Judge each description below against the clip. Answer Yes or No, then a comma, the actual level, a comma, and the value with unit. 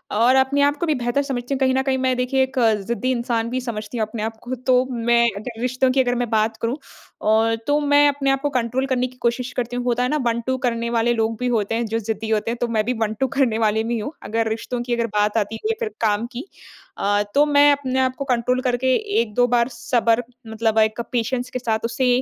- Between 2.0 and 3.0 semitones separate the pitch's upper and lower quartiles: Yes, narrow, 2.4 semitones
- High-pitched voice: Yes, high, 240 Hz